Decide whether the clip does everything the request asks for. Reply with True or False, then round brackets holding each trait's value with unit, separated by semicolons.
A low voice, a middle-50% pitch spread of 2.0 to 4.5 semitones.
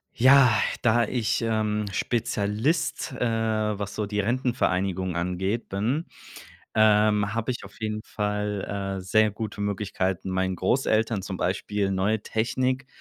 True (105 Hz; 2.4 semitones)